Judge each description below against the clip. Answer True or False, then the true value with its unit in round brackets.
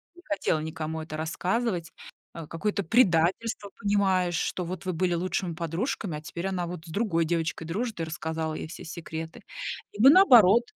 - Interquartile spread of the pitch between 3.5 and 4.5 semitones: True (3.8 semitones)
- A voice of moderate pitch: True (175 Hz)